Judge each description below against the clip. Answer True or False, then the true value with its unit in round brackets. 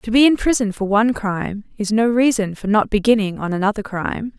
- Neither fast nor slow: False (220 wpm)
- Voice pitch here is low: False (215 Hz)